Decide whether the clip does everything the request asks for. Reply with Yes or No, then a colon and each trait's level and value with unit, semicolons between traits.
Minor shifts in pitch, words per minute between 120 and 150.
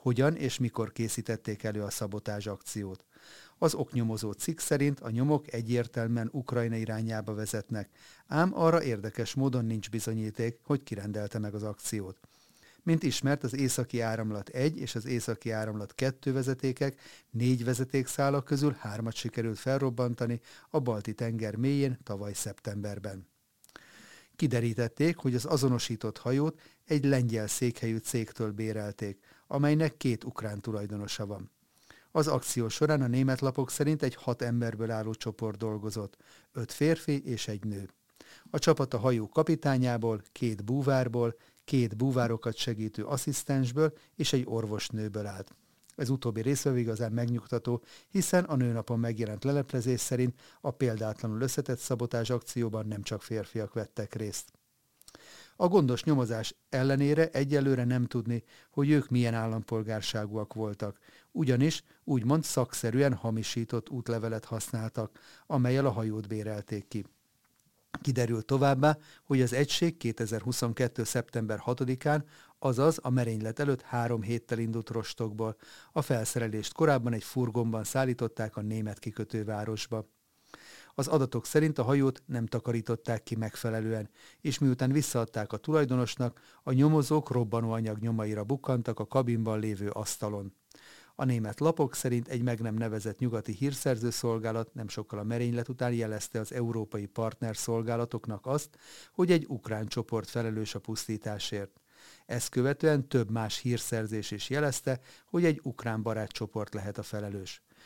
No: average, 3.4 semitones; average, 130 wpm